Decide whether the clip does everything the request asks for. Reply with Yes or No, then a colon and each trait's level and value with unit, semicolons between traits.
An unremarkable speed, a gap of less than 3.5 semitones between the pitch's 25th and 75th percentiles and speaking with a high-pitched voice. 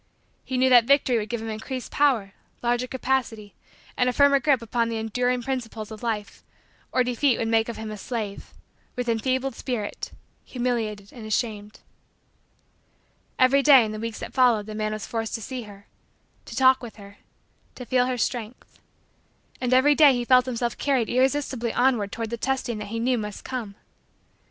Yes: average, 180 wpm; average, 2.9 semitones; high, 240 Hz